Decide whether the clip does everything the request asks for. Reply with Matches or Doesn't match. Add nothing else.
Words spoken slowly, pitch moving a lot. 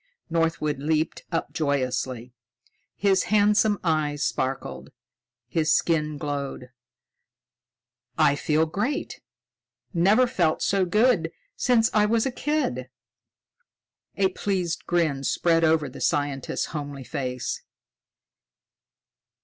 Matches